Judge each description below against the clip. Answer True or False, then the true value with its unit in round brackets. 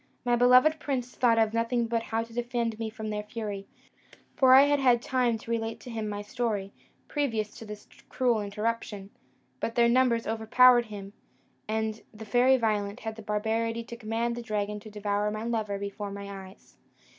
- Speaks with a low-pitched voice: False (225 Hz)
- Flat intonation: True (2.2 semitones)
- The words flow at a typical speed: True (185 wpm)